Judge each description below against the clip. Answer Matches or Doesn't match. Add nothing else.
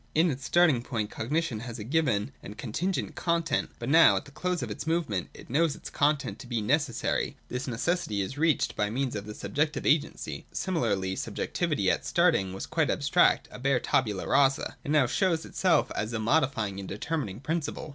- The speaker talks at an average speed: Matches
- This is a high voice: Doesn't match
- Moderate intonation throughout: Doesn't match